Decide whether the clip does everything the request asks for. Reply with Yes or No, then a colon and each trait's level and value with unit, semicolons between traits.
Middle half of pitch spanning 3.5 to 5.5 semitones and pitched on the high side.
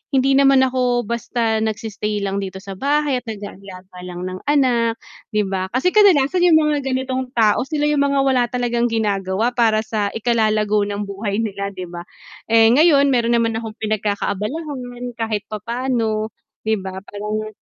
Yes: average, 3.9 semitones; high, 225 Hz